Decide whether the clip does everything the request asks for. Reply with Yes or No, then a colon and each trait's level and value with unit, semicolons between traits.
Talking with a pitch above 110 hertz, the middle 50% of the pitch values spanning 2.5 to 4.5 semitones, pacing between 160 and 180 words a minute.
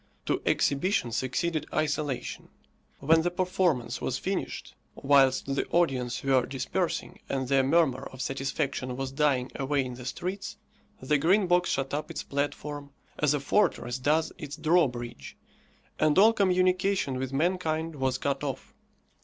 No: medium, 140 Hz; average, 3.9 semitones; average, 145 wpm